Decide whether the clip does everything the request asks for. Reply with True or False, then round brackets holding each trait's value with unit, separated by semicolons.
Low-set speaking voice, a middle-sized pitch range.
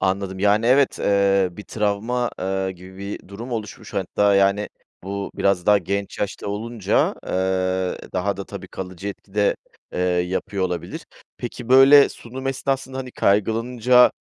True (100 Hz; 3.6 semitones)